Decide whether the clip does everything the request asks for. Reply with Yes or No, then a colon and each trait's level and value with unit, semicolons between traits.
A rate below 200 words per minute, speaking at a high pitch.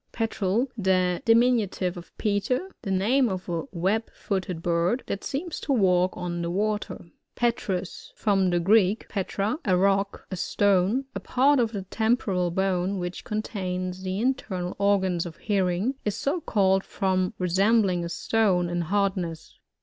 Yes: average, 155 wpm; high, 195 Hz